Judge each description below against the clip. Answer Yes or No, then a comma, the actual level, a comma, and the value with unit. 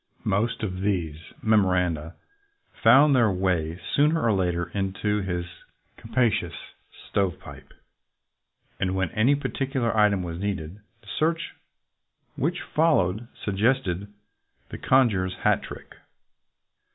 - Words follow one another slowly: Yes, slow, 115 wpm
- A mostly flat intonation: No, average, 4.7 semitones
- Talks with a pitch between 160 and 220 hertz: No, low, 100 Hz